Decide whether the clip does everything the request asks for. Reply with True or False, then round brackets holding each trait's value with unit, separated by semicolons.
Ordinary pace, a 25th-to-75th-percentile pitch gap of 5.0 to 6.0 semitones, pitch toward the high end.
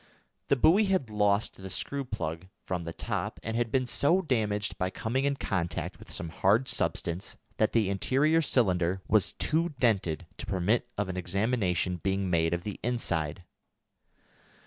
False (165 wpm; 5.5 semitones; 105 Hz)